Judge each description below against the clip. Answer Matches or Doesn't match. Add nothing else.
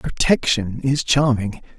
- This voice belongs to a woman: Doesn't match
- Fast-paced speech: Doesn't match